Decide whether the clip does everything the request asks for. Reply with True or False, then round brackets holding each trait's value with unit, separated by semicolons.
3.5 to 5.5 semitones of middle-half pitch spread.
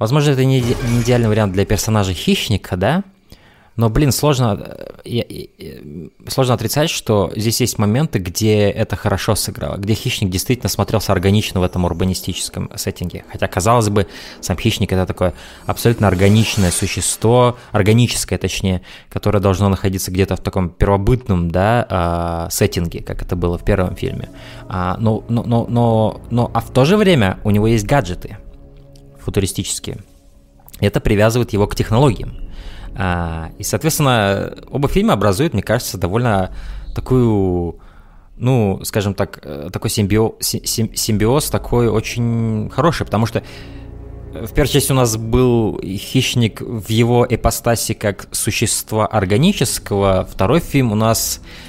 True (3.9 semitones)